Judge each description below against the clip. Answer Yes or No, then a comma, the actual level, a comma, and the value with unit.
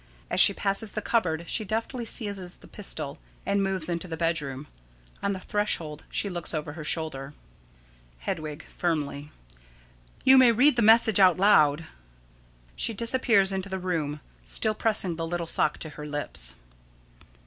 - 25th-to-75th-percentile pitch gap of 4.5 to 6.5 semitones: Yes, wide, 5.4 semitones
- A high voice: No, medium, 180 Hz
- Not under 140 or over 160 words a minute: Yes, average, 155 wpm